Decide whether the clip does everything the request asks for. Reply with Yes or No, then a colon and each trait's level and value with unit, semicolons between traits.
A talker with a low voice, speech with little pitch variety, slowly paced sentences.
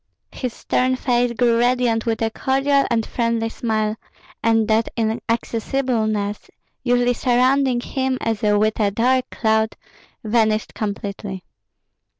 No: high, 230 Hz; narrow, 2.3 semitones; slow, 120 wpm